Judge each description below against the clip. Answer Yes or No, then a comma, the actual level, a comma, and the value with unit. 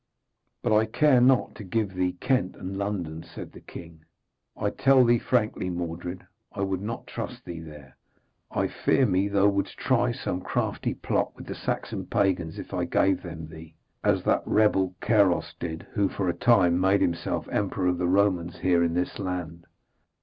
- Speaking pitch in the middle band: No, very low, 95 Hz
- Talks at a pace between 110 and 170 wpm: No, average, 185 wpm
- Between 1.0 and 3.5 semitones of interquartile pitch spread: Yes, average, 3.0 semitones